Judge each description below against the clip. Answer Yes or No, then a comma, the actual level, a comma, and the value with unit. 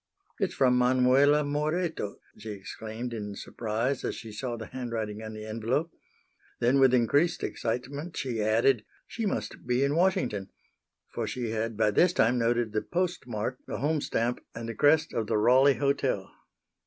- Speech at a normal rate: Yes, average, 165 wpm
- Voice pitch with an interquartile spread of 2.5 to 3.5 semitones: No, average, 4.3 semitones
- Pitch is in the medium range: No, low, 125 Hz